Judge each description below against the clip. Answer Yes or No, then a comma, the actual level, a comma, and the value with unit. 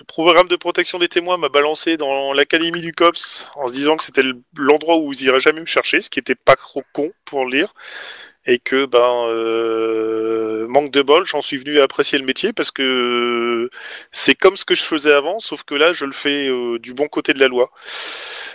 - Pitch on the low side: No, medium, 145 Hz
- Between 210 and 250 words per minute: Yes, fast, 220 wpm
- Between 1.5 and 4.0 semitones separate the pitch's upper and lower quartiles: No, average, 4.6 semitones